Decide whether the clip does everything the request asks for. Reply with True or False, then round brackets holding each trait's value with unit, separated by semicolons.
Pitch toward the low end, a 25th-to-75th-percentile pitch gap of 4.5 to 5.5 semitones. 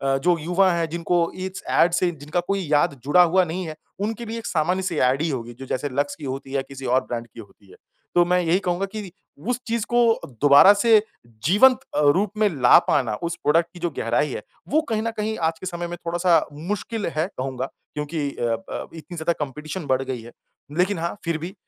False (170 Hz; 4.8 semitones)